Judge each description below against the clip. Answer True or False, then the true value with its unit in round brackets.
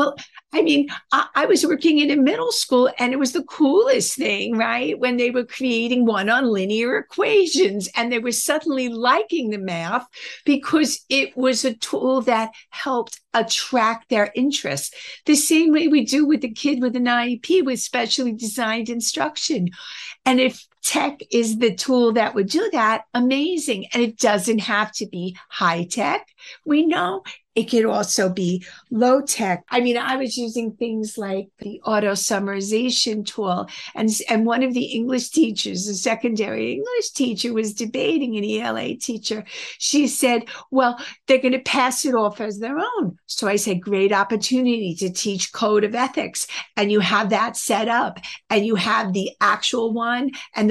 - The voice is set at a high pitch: True (240 Hz)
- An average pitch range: True (3.7 semitones)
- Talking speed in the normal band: True (175 wpm)